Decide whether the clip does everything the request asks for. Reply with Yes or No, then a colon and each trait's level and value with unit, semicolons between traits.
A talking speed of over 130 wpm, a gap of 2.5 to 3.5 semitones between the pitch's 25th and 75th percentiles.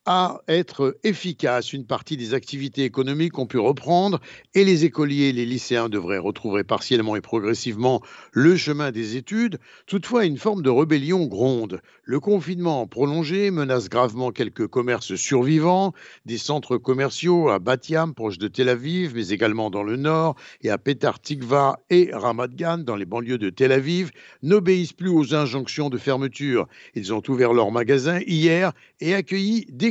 No: average, 165 wpm; wide, 5.6 semitones